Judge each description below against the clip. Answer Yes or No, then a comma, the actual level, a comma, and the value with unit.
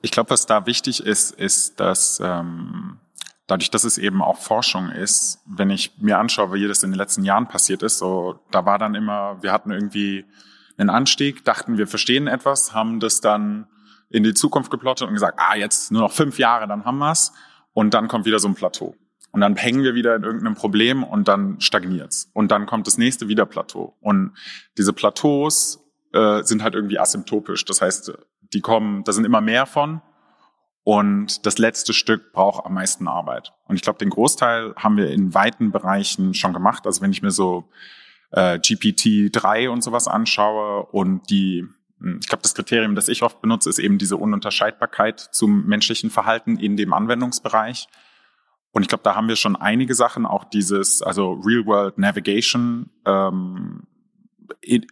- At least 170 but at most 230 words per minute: Yes, average, 185 wpm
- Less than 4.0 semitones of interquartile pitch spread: No, average, 4.3 semitones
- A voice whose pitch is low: Yes, low, 110 Hz